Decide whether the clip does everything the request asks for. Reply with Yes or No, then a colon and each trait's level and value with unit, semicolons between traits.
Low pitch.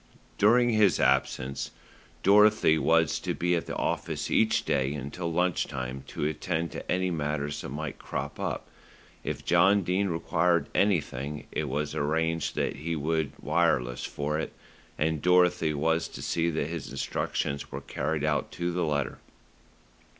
Yes: very low, 80 Hz